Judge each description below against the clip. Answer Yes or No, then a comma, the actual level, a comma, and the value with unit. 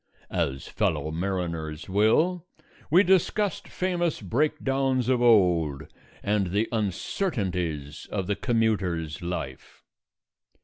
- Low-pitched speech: Yes, low, 100 Hz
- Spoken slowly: Yes, slow, 95 wpm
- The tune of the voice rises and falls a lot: Yes, wide, 7.8 semitones